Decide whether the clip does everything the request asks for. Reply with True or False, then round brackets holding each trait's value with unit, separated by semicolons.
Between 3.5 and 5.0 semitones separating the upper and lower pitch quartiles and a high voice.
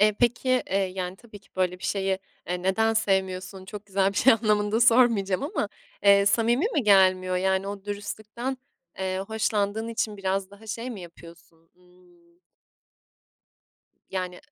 False (2.9 semitones; 200 Hz)